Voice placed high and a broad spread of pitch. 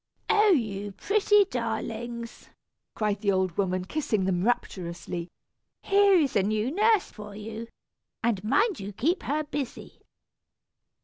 Yes: high, 225 Hz; wide, 7.5 semitones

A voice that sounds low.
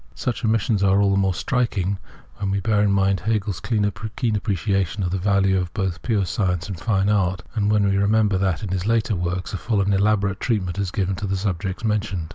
Yes: low, 100 Hz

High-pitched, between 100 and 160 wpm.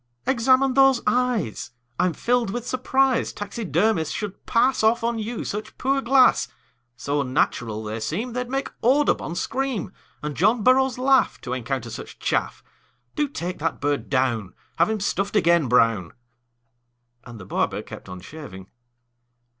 Yes: high, 210 Hz; average, 145 wpm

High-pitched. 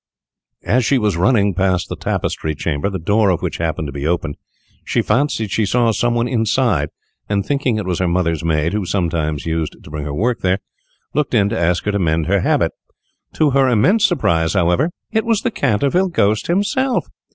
No: low, 100 Hz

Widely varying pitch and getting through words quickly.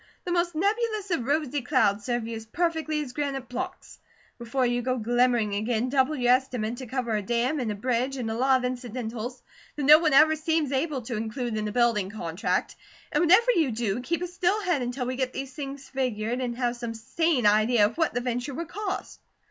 No: average, 4.3 semitones; fast, 215 wpm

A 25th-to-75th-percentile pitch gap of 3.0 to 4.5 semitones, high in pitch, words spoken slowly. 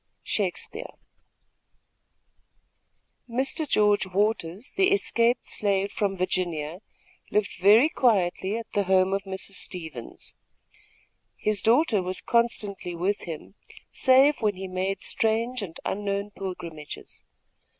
Yes: average, 3.7 semitones; high, 200 Hz; slow, 110 wpm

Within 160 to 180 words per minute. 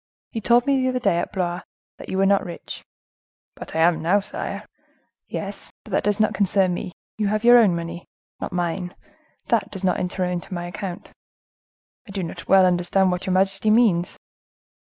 No: average, 195 wpm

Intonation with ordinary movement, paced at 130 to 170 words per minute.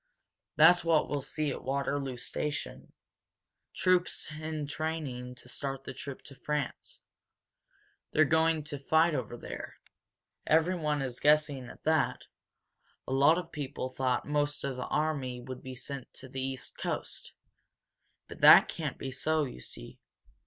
Yes: average, 3.0 semitones; average, 145 wpm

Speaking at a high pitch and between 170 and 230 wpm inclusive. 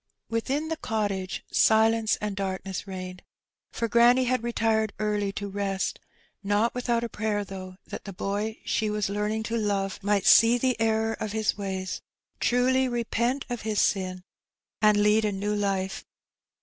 No: high, 210 Hz; average, 160 wpm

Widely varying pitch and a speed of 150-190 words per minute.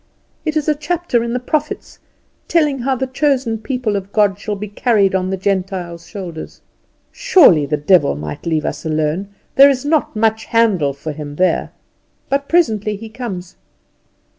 Yes: wide, 6.8 semitones; average, 170 wpm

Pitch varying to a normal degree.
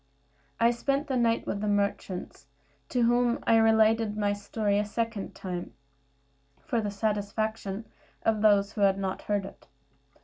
No: narrow, 2.1 semitones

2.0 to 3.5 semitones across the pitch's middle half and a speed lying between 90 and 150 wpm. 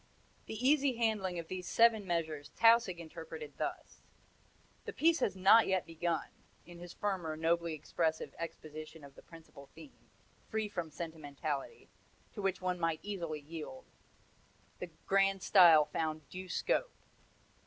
No: average, 4.3 semitones; average, 140 wpm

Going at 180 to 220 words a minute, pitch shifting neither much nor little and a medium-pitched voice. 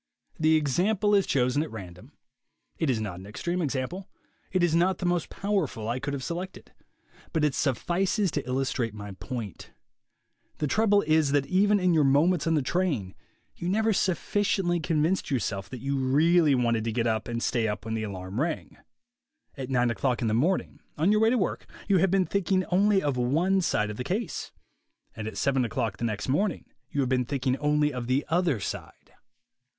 No: average, 195 wpm; wide, 6.8 semitones; medium, 145 Hz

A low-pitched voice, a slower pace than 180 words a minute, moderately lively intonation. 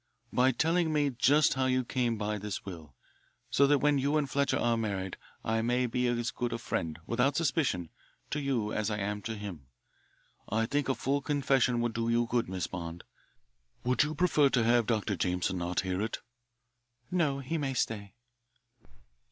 No: low, 120 Hz; average, 185 wpm; average, 4.9 semitones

